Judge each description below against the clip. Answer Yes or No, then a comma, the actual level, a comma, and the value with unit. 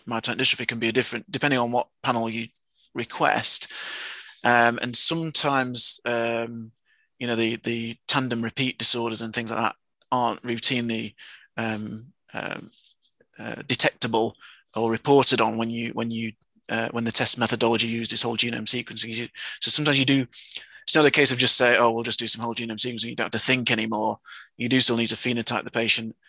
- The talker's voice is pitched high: No, low, 115 Hz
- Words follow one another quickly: No, average, 185 wpm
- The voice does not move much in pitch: Yes, narrow, 1.5 semitones